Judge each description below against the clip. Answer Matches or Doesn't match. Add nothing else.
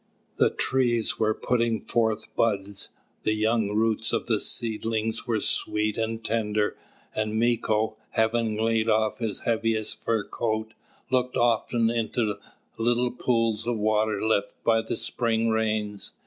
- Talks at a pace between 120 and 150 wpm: Matches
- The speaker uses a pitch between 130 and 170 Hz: Doesn't match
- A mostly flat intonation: Matches